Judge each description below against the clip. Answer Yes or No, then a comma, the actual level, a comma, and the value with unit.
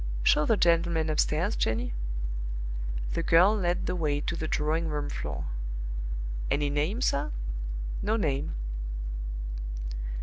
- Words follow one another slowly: Yes, slow, 115 wpm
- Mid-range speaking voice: Yes, medium, 160 Hz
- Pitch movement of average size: Yes, average, 3.1 semitones